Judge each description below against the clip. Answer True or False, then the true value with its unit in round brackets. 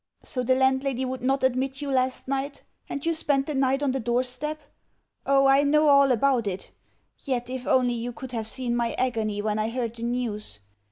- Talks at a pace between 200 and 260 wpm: True (205 wpm)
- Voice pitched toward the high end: True (260 Hz)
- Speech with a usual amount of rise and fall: False (2.3 semitones)